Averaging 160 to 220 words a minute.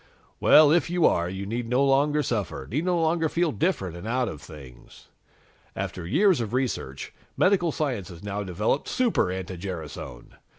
Yes: average, 170 wpm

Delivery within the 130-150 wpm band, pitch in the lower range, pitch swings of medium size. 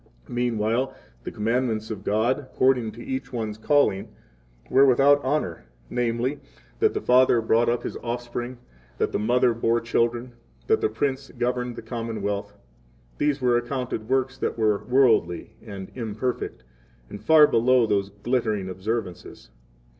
Yes: average, 140 wpm; low, 120 Hz; average, 3.1 semitones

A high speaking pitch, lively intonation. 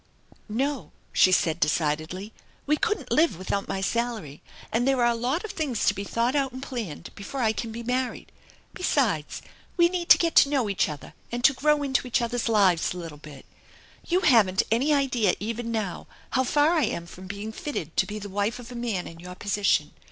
Yes: high, 230 Hz; wide, 5.8 semitones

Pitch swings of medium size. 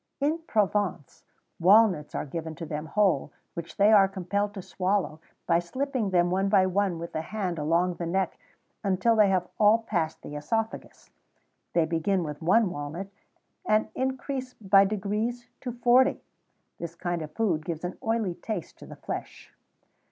Yes: average, 4.3 semitones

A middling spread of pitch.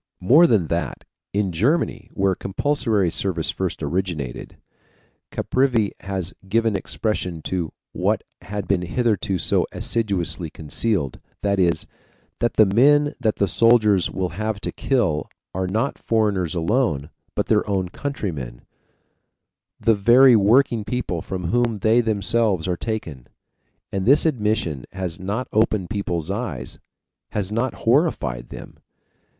Yes: average, 4.5 semitones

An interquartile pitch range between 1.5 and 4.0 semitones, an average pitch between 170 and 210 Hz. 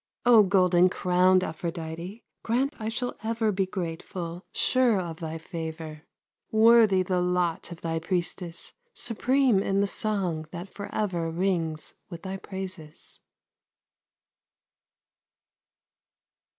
Yes: average, 3.6 semitones; medium, 185 Hz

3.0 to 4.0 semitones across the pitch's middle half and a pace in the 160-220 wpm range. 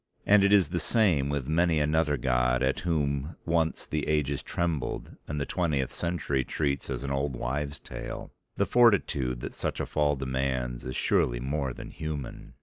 Yes: average, 3.4 semitones; average, 175 wpm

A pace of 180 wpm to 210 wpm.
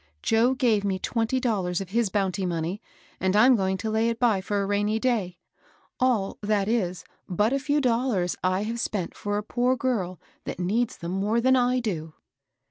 Yes: average, 195 wpm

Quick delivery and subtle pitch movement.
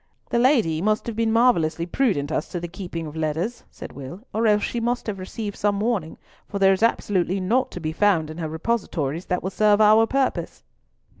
No: fast, 210 wpm; average, 5.3 semitones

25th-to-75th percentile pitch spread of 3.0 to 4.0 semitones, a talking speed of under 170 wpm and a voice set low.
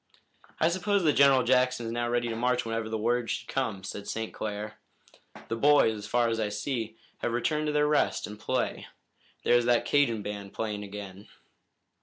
No: average, 3.3 semitones; average, 195 wpm; low, 115 Hz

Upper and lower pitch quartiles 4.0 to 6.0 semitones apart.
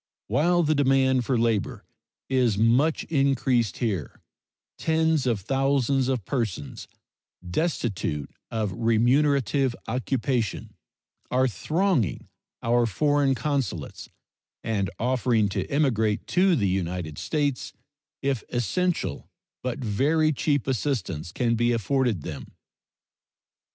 Yes: average, 4.3 semitones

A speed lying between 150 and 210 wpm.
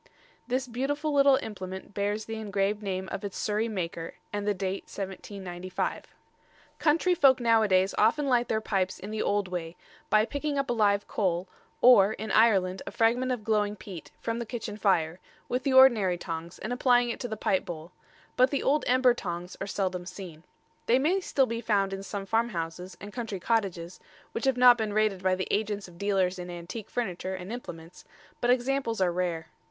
Yes: average, 190 wpm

